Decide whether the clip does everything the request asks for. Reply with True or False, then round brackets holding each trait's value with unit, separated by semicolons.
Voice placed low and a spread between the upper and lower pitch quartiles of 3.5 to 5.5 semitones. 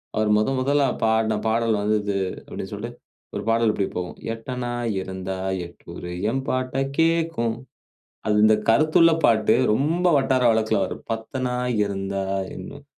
True (115 Hz; 3.9 semitones)